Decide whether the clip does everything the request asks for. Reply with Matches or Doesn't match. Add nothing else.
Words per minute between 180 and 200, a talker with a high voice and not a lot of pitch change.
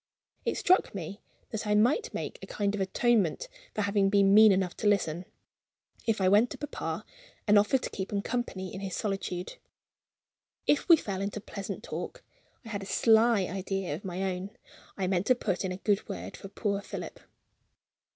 Matches